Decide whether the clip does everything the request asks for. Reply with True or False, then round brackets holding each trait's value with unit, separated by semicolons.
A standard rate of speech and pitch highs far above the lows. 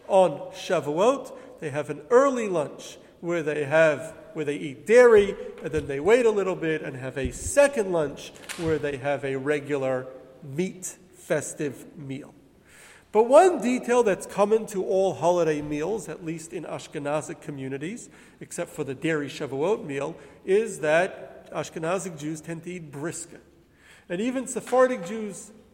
True (155 wpm; 6.2 semitones)